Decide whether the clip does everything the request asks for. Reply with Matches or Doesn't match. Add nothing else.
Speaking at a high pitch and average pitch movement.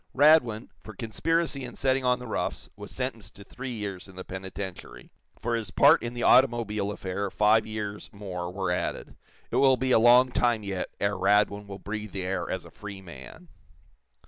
Doesn't match